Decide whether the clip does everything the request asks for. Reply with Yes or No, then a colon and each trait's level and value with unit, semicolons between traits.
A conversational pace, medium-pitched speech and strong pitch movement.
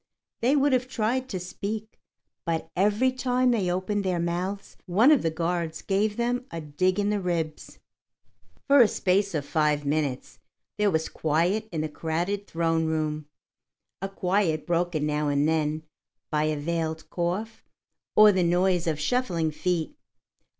No: average, 155 wpm; medium, 175 Hz; average, 4.6 semitones